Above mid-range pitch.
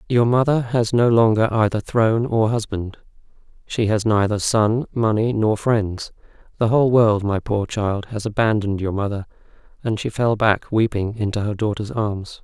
No: low, 110 Hz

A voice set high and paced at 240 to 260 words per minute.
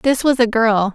Yes: high, 235 Hz; fast, 255 wpm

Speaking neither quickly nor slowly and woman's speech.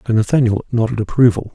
No: average, 155 wpm; male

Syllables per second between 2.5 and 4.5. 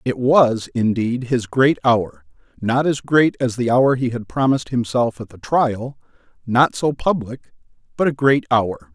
Yes: 4.3 syllables/s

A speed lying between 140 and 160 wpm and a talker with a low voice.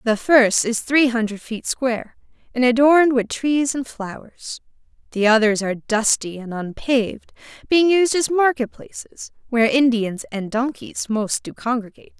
No: average, 150 wpm; high, 245 Hz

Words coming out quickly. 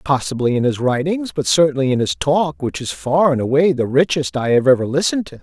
Yes: fast, 220 wpm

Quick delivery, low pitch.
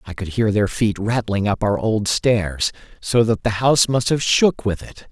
Yes: fast, 225 wpm; low, 110 Hz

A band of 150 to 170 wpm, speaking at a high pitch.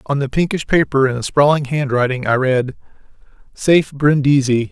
No: average, 155 wpm; medium, 140 Hz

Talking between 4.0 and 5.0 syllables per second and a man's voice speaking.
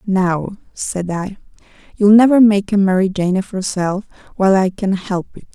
No: 4.7 syllables/s; female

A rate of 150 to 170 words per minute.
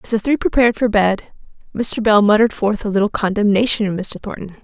No: fast, 205 wpm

